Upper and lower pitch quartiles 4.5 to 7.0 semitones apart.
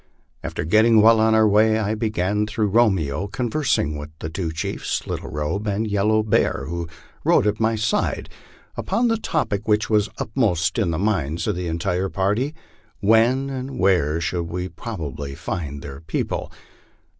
Yes: average, 4.8 semitones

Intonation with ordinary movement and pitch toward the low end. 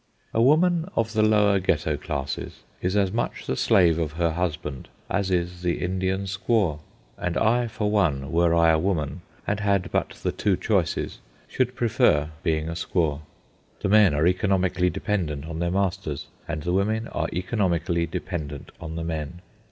Yes: average, 4.0 semitones; very low, 90 Hz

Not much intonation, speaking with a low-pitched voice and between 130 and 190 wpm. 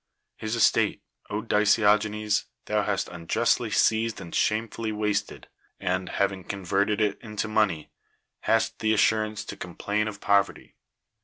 Yes: narrow, 1.5 semitones; low, 105 Hz; slow, 135 wpm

